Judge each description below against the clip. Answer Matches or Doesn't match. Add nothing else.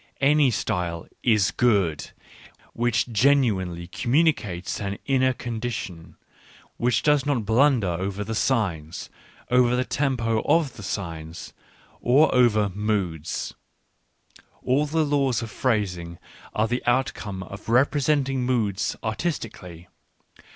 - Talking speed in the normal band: Doesn't match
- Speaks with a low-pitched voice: Matches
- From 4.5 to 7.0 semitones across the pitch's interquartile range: Matches